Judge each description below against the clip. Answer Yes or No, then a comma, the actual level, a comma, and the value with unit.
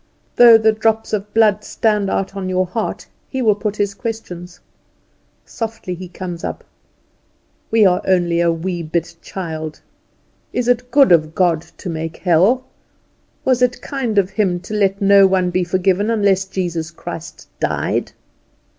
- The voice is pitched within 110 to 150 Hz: No, high, 195 Hz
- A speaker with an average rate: Yes, average, 155 wpm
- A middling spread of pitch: Yes, average, 3.7 semitones